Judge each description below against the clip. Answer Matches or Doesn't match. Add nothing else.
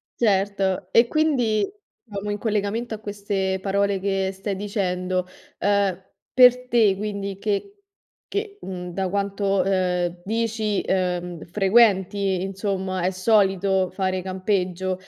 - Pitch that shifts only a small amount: Matches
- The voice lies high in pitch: Matches